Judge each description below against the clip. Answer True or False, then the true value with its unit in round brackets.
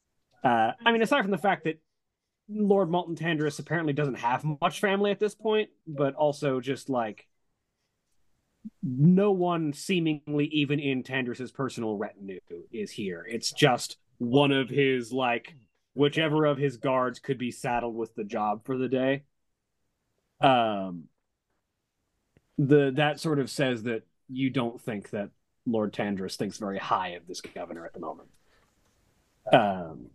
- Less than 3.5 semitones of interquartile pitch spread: False (4.6 semitones)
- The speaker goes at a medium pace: True (150 wpm)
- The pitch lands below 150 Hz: True (140 Hz)